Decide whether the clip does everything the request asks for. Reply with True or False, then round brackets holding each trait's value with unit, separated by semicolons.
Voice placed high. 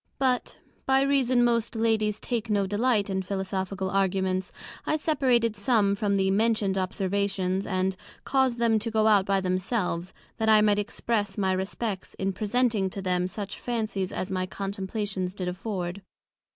True (200 Hz)